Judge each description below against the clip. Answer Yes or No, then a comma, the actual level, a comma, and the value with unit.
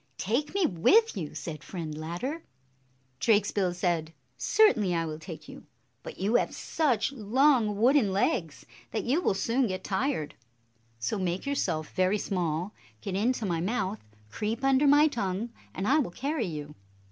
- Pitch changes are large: Yes, wide, 6.9 semitones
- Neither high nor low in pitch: No, high, 205 Hz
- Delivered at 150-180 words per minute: Yes, average, 160 wpm